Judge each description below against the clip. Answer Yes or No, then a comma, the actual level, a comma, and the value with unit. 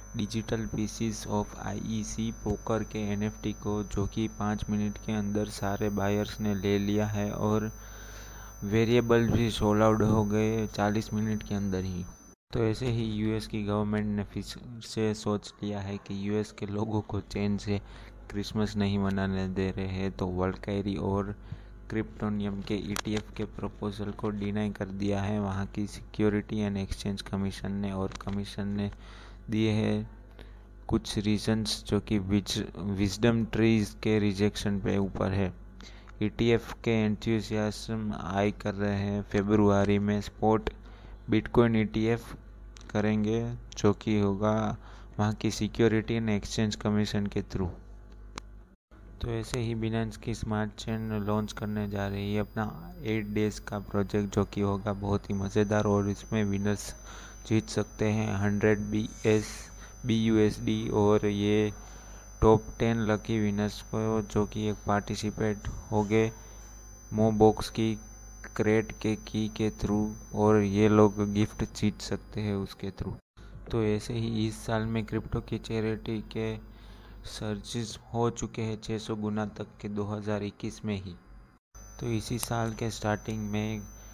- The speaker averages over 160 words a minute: No, average, 150 wpm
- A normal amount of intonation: No, narrow, 1.2 semitones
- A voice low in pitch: Yes, low, 105 Hz